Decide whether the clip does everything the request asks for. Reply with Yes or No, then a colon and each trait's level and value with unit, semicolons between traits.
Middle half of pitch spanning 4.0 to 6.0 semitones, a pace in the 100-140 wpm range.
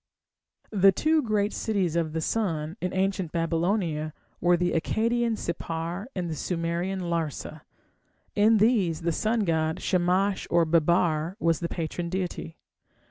No: average, 3.2 semitones; slow, 135 wpm